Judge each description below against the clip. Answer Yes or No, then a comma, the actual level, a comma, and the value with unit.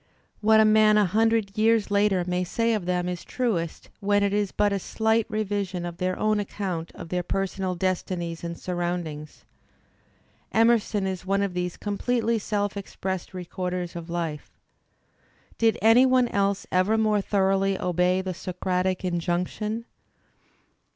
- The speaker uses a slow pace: No, average, 155 wpm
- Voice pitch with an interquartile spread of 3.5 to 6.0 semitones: No, average, 3.0 semitones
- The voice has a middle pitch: No, high, 195 Hz